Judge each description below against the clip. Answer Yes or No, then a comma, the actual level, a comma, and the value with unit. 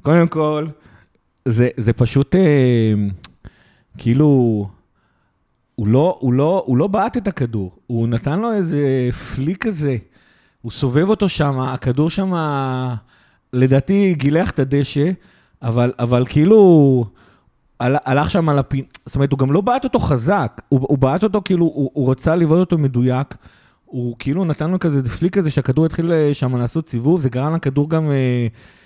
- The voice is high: No, medium, 140 Hz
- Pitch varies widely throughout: No, average, 4.7 semitones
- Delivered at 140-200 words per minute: Yes, fast, 150 wpm